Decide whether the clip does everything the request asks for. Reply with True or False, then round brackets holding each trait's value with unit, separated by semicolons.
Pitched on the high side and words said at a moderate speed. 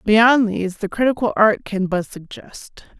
True (210 Hz; 160 wpm)